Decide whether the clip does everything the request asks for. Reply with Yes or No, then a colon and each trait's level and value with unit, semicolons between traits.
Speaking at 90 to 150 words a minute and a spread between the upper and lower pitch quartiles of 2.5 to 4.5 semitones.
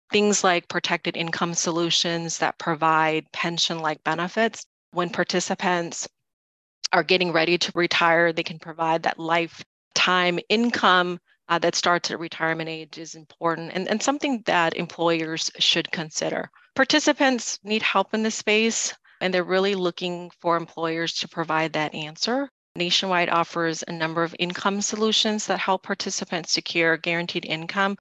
Yes: average, 145 wpm; average, 2.8 semitones